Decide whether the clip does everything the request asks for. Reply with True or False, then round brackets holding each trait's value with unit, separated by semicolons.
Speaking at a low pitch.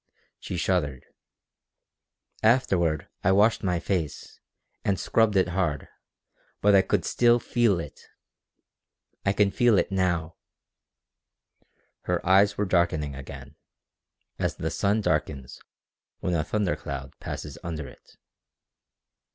True (95 Hz)